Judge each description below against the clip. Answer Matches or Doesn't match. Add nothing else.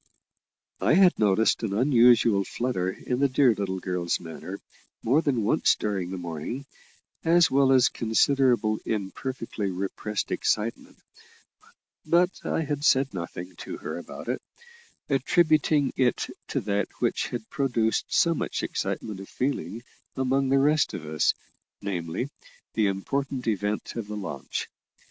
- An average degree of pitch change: Doesn't match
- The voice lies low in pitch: Matches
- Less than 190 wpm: Matches